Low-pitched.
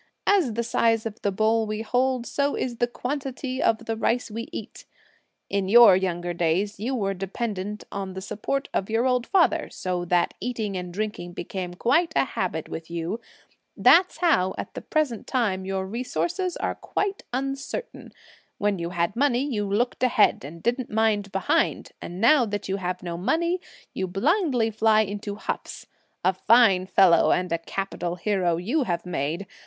No: high, 210 Hz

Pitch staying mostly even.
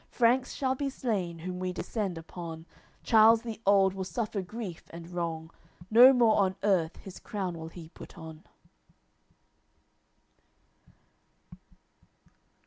No: average, 4.8 semitones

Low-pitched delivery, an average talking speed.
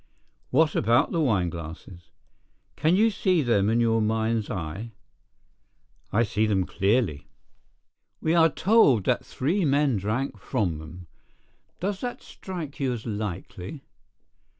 No: low, 115 Hz; slow, 125 wpm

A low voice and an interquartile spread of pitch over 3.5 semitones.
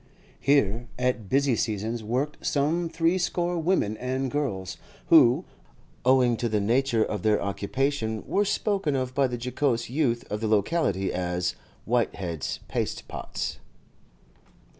Yes: low, 125 Hz; average, 5.0 semitones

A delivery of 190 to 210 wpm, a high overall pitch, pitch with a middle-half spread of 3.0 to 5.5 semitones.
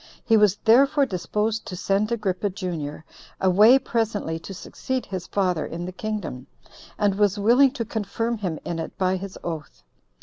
No: average, 165 wpm; high, 200 Hz; average, 3.6 semitones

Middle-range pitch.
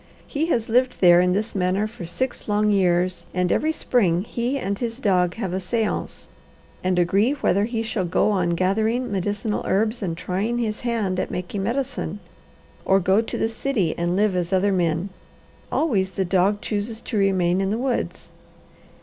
No: high, 200 Hz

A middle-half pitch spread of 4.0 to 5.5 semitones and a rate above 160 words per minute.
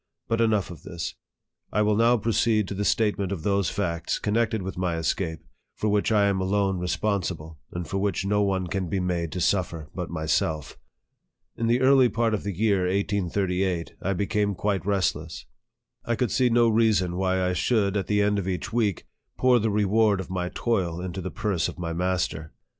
No: average, 2.9 semitones; average, 195 wpm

